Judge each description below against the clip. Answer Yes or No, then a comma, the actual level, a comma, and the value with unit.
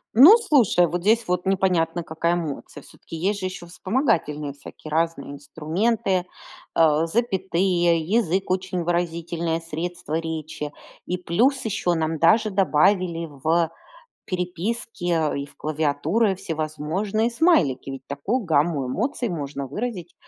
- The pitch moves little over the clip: No, average, 3.7 semitones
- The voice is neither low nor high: Yes, medium, 175 Hz